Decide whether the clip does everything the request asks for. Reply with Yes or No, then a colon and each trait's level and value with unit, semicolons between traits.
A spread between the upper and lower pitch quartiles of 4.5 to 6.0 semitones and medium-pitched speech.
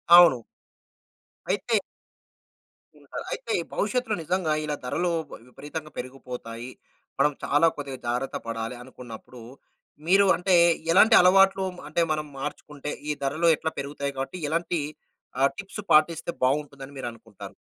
Yes: average, 5.0 semitones; medium, 150 Hz